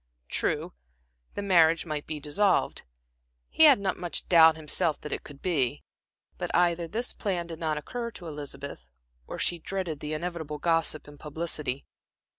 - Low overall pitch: No, medium, 165 Hz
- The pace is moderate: Yes, average, 160 wpm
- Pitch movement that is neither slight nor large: Yes, average, 3.0 semitones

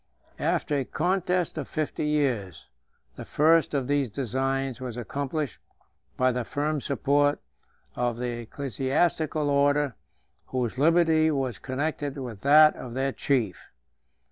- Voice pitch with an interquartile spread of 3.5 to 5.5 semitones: No, average, 3.0 semitones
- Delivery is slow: Yes, slow, 125 wpm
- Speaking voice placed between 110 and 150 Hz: Yes, medium, 140 Hz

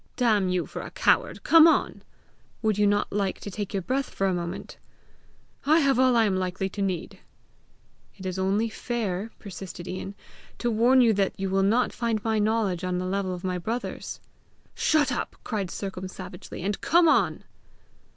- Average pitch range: Yes, average, 3.7 semitones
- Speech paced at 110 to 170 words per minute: No, average, 185 wpm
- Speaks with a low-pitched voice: No, high, 200 Hz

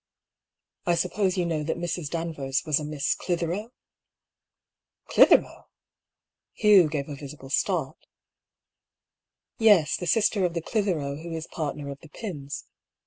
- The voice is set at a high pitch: No, medium, 165 Hz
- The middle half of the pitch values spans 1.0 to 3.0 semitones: No, average, 3.6 semitones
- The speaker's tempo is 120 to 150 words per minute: Yes, average, 140 wpm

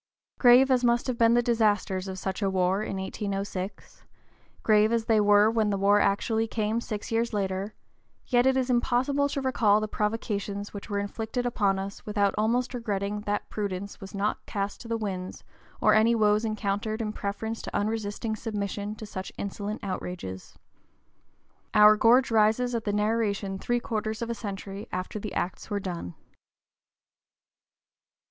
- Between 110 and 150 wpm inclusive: No, average, 165 wpm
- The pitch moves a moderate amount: No, narrow, 2.3 semitones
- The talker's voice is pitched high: Yes, high, 210 Hz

